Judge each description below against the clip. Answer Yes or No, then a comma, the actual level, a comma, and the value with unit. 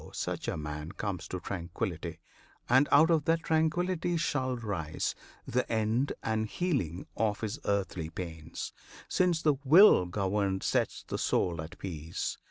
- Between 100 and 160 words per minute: Yes, average, 145 wpm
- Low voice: Yes, low, 105 Hz